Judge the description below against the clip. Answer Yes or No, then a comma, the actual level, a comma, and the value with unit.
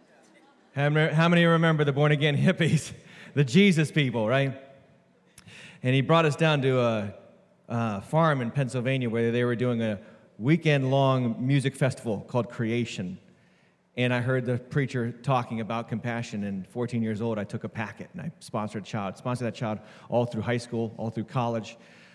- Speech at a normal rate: Yes, average, 170 wpm